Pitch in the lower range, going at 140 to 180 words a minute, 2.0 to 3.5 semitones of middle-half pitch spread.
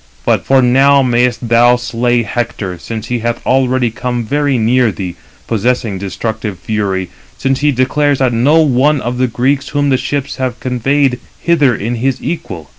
Yes: low, 125 Hz; average, 165 wpm; average, 2.7 semitones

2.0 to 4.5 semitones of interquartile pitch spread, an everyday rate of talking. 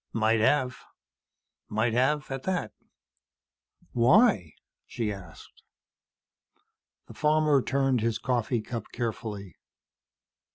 No: average, 4.0 semitones; slow, 90 wpm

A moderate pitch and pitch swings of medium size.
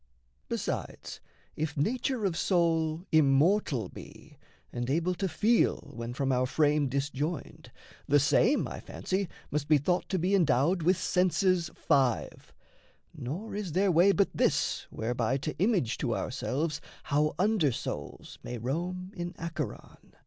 Yes: medium, 160 Hz; average, 5.0 semitones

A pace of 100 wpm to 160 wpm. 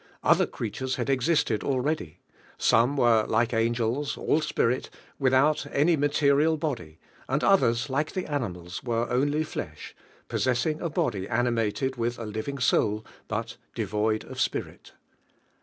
Yes: average, 140 wpm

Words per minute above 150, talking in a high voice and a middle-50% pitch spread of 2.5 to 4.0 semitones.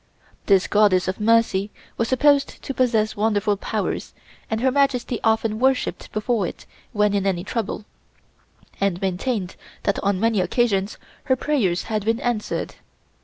No: average, 145 wpm; high, 215 Hz; average, 3.4 semitones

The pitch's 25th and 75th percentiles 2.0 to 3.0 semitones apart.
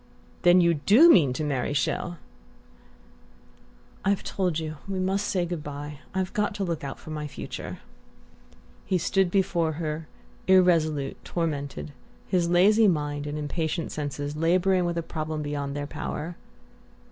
No: average, 3.8 semitones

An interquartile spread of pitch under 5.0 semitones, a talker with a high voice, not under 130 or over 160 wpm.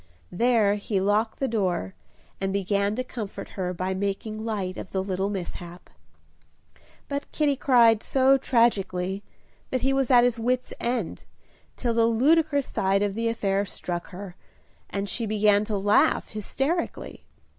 Yes: average, 4.0 semitones; high, 210 Hz; average, 150 wpm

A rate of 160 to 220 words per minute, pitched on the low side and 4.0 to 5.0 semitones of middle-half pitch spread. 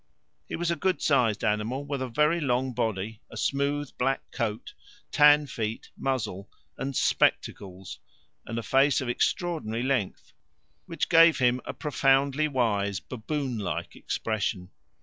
No: average, 140 wpm; low, 130 Hz; average, 4.7 semitones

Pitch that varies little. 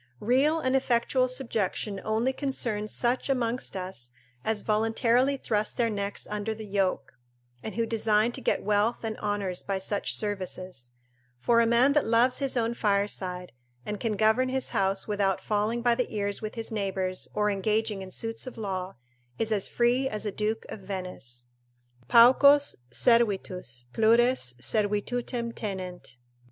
No: average, 3.2 semitones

